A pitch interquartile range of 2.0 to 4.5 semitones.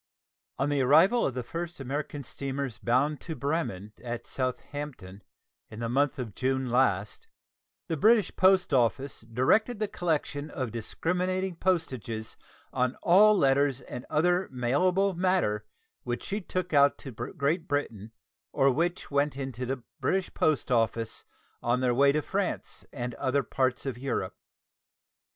No: average, 5.3 semitones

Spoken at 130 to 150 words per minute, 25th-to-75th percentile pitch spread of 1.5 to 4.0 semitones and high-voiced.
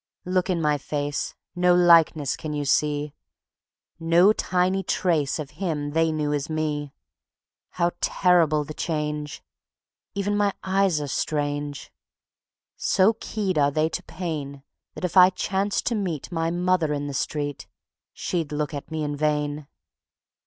No: average, 145 wpm; average, 3.5 semitones; medium, 155 Hz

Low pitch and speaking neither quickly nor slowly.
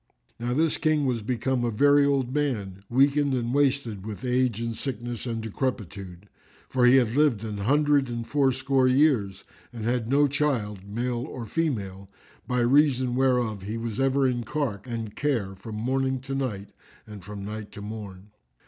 Yes: low, 120 Hz; average, 170 wpm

